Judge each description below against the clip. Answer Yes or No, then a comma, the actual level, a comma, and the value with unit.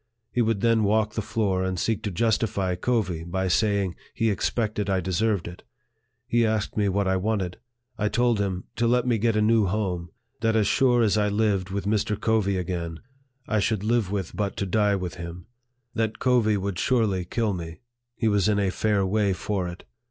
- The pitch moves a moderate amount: Yes, average, 3.0 semitones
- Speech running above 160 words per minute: Yes, average, 200 wpm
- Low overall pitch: Yes, low, 105 Hz